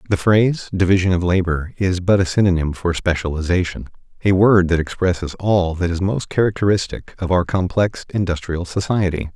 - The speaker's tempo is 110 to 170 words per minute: Yes, average, 160 wpm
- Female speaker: No, male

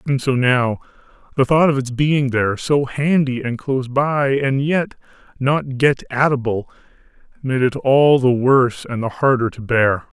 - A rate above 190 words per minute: No, average, 175 wpm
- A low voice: Yes, low, 130 Hz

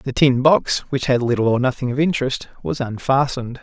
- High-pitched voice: No, low, 130 Hz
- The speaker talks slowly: No, average, 200 wpm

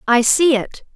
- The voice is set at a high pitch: Yes, very high, 260 Hz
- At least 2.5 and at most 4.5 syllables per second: Yes, 4.0 syllables/s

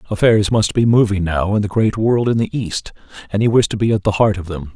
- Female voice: No, male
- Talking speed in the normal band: No, fast, 275 wpm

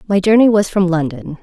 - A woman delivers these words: Yes, female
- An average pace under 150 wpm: No, fast, 210 wpm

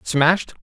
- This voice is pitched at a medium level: Yes, medium, 165 Hz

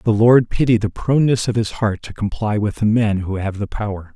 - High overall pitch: No, low, 110 Hz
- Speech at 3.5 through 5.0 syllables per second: No, 5.5 syllables/s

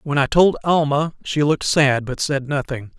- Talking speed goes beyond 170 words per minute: Yes, average, 200 wpm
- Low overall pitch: No, medium, 145 Hz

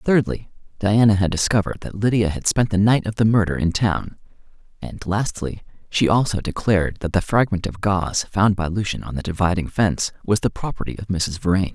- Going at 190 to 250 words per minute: Yes, average, 195 wpm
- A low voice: Yes, very low, 95 Hz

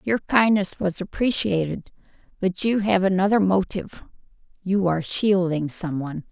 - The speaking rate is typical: No, slow, 115 wpm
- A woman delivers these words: Yes, female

